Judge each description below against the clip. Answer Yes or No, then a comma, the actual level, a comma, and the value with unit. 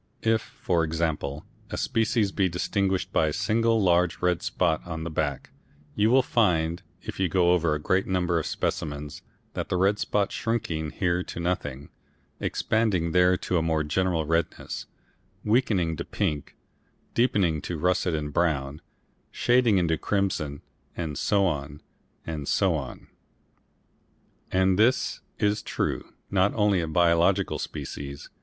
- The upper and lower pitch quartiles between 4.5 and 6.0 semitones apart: No, average, 3.7 semitones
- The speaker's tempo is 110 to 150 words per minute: Yes, average, 145 wpm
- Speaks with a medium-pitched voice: No, very low, 90 Hz